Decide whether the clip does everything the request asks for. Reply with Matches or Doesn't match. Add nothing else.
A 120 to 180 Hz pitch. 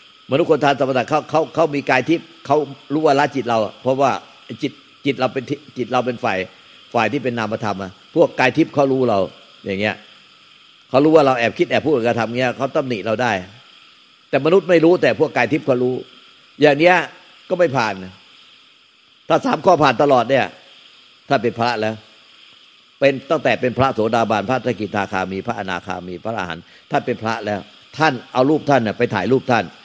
Matches